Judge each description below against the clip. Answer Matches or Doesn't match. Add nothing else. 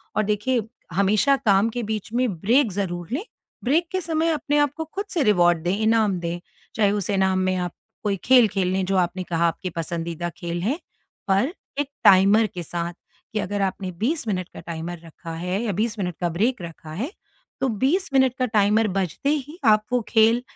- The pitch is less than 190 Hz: Doesn't match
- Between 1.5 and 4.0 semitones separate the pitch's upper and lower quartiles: Doesn't match